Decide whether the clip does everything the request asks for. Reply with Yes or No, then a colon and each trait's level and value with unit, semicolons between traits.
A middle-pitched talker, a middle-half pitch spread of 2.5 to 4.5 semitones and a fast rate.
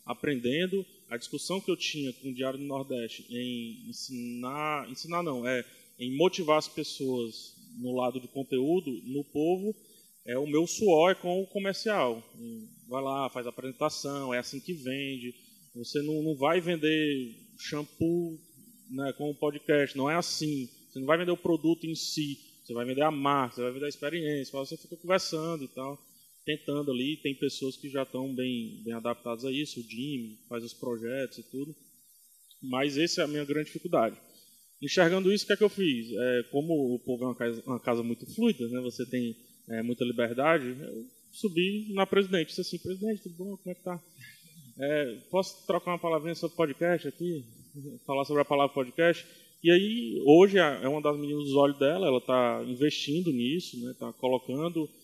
No: medium, 145 Hz; average, 5.1 semitones; fast, 190 wpm